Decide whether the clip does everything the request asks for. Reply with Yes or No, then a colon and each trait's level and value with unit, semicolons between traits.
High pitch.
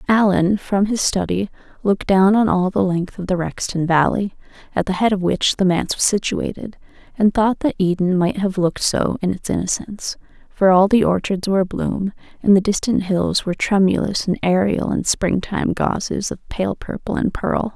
Yes: high, 195 Hz